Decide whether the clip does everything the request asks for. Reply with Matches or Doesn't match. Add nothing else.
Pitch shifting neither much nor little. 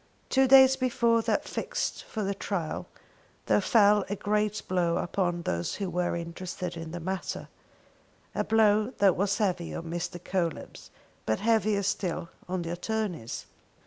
Matches